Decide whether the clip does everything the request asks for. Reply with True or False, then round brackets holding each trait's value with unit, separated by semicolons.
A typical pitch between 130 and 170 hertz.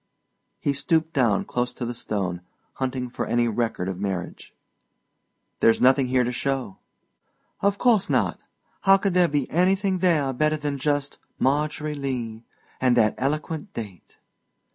True (135 Hz)